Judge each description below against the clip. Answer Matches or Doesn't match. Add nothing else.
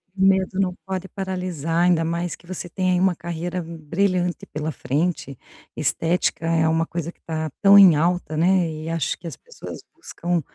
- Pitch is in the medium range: Matches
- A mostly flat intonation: Matches